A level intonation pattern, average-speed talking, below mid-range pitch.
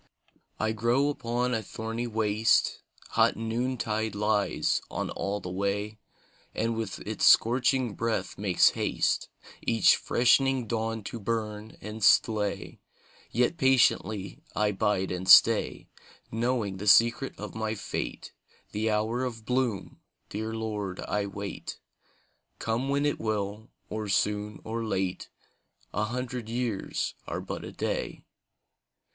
No: narrow, 2.2 semitones; slow, 130 wpm; low, 110 Hz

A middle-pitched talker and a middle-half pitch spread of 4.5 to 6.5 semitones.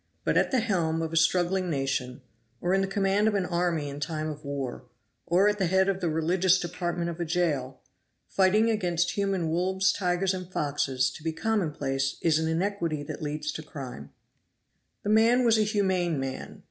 No: medium, 175 Hz; average, 3.9 semitones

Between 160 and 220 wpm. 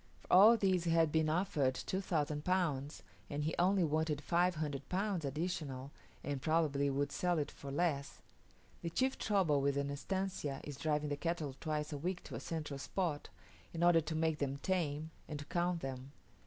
Yes: average, 180 wpm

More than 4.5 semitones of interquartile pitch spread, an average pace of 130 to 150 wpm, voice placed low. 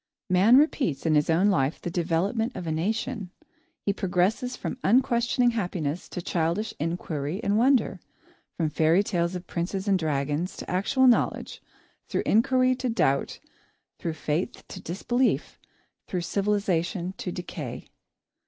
No: average, 5.3 semitones; average, 140 wpm; medium, 185 Hz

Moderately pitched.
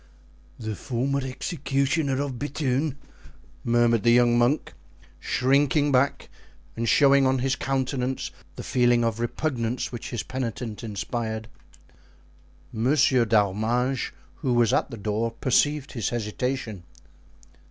No: low, 125 Hz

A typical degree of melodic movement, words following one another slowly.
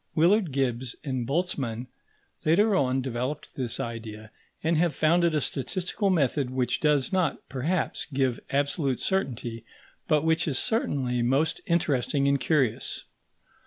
Yes: average, 4.5 semitones; slow, 130 wpm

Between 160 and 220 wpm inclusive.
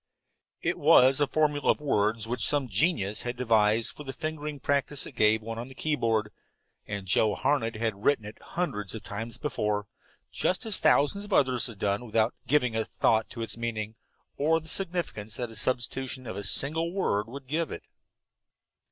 Yes: average, 185 wpm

